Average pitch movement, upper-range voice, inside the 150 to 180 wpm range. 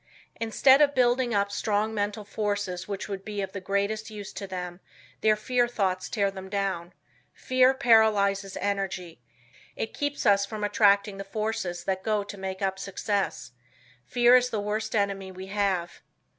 No: narrow, 2.2 semitones; high, 200 Hz; average, 165 wpm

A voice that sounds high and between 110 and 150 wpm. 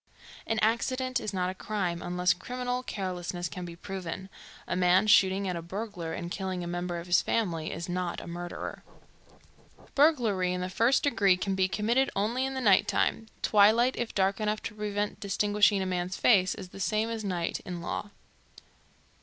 No: high, 195 Hz; average, 185 wpm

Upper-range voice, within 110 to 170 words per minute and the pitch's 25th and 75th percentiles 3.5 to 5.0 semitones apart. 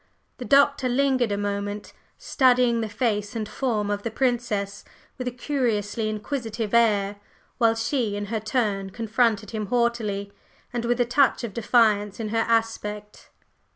No: high, 225 Hz; average, 155 wpm; average, 2.8 semitones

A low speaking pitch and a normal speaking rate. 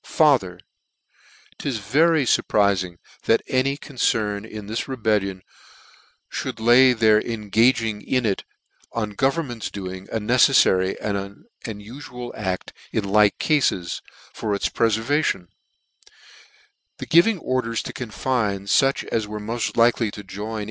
No: low, 110 Hz; slow, 130 wpm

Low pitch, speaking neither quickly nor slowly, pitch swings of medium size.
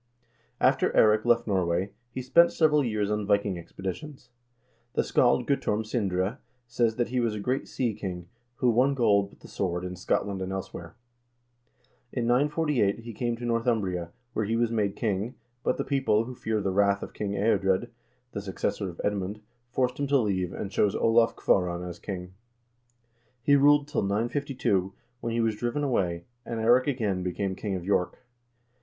Yes: low, 110 Hz; average, 175 wpm; average, 4.1 semitones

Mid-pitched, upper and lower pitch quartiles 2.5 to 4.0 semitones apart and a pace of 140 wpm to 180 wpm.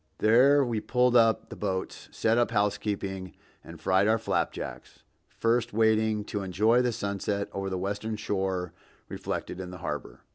No: low, 105 Hz; average, 2.9 semitones; average, 155 wpm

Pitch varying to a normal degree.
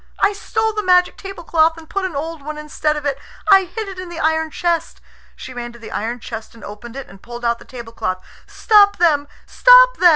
No: wide, 7.2 semitones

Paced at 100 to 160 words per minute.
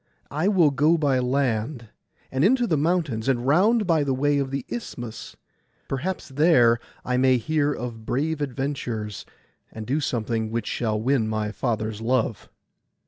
Yes: average, 155 wpm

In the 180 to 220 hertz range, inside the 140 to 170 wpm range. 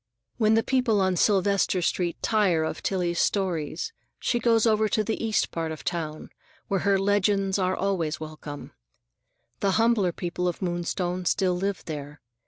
Yes: high, 190 Hz; average, 160 wpm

